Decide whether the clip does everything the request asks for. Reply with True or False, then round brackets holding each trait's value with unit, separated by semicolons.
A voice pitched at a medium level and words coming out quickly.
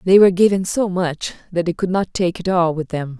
True (180 Hz; 265 wpm)